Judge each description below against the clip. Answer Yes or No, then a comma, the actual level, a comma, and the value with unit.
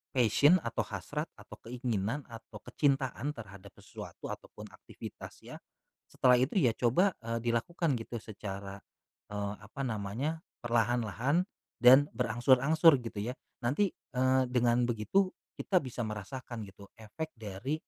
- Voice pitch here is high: No, low, 120 Hz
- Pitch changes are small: No, average, 4.1 semitones